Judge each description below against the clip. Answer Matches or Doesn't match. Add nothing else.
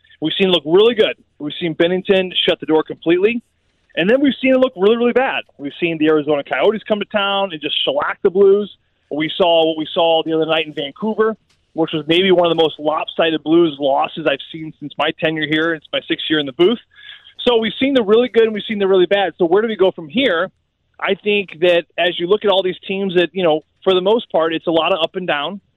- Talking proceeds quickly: Matches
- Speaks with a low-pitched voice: Doesn't match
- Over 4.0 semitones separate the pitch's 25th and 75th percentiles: Matches